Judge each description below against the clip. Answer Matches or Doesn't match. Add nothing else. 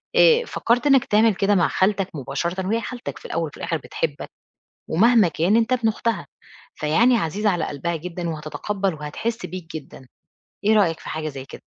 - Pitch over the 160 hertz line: Matches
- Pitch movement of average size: Doesn't match